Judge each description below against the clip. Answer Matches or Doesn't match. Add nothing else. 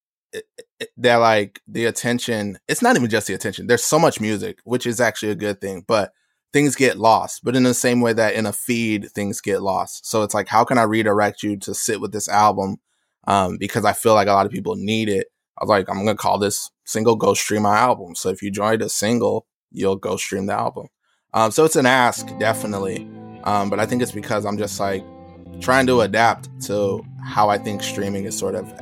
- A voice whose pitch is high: Doesn't match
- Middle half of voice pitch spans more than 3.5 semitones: Doesn't match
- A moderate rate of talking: Doesn't match